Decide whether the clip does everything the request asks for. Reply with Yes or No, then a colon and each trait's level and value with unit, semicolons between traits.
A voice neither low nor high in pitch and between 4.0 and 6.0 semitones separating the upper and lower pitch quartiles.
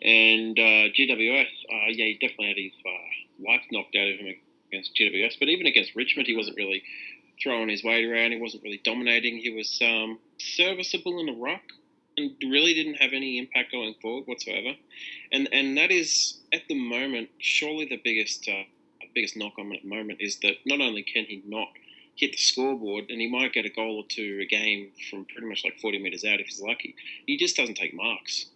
No: low, 115 Hz; average, 4.5 semitones